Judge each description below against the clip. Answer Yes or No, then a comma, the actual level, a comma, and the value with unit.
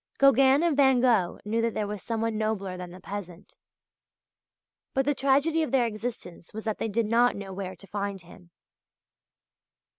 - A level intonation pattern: No, average, 4.9 semitones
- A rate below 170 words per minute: No, average, 175 wpm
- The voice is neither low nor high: No, high, 220 Hz